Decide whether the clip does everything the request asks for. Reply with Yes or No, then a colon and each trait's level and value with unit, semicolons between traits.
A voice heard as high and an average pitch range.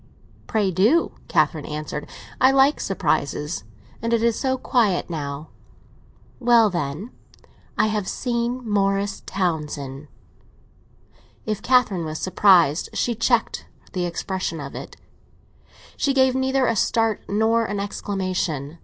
No: high, 200 Hz; wide, 6.0 semitones